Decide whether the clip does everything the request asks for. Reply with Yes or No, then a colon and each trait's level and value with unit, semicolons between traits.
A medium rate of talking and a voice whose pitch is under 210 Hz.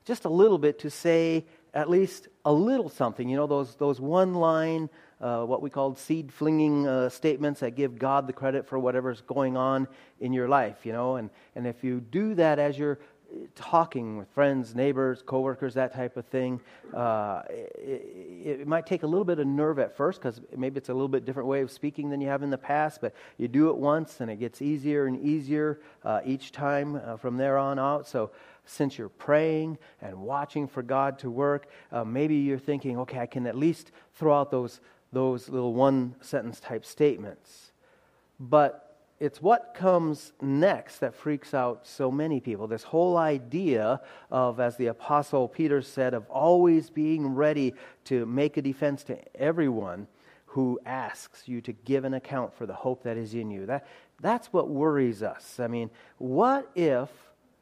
Yes: average, 195 wpm; medium, 140 Hz